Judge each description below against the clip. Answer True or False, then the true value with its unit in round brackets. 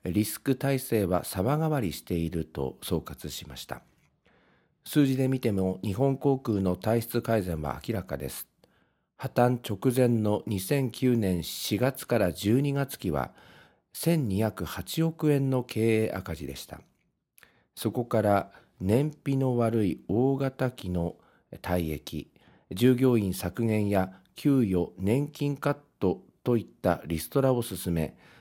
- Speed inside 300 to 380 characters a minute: False (220 characters per minute)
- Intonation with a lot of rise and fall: True (6.4 semitones)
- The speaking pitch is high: False (110 Hz)